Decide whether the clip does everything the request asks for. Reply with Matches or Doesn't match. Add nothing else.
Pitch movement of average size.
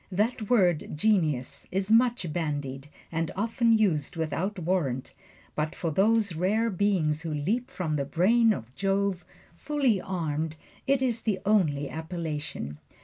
Doesn't match